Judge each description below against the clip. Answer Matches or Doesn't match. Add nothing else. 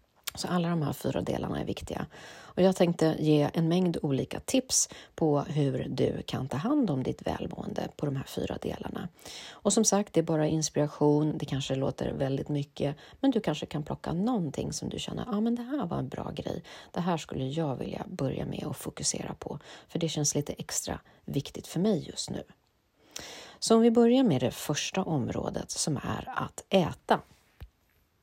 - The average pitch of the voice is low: Doesn't match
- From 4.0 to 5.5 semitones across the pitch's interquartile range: Matches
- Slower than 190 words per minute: Doesn't match